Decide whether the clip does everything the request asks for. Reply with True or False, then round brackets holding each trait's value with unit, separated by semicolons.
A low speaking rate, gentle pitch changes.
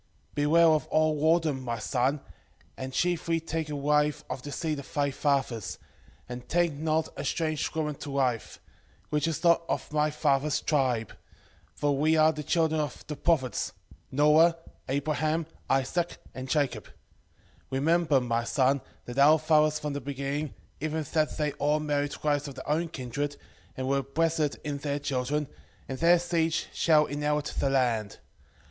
False (165 wpm; 2.3 semitones)